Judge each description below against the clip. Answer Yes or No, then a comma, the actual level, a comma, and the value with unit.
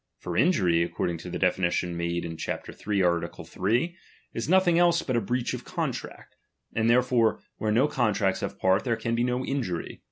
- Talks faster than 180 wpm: Yes, average, 195 wpm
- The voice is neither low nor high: No, low, 110 Hz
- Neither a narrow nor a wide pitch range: No, wide, 6.1 semitones